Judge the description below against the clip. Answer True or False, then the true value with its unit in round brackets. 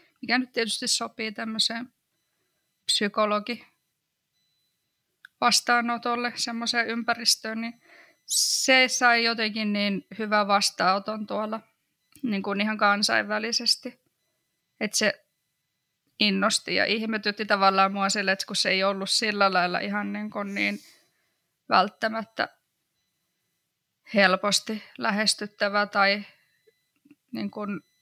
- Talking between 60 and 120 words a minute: True (100 wpm)